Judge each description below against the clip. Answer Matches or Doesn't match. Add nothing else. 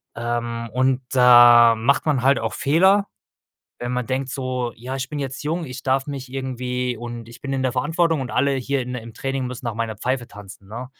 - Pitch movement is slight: Matches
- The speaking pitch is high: Doesn't match